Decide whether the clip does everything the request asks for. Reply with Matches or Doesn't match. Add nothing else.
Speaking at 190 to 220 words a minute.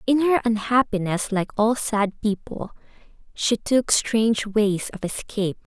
Doesn't match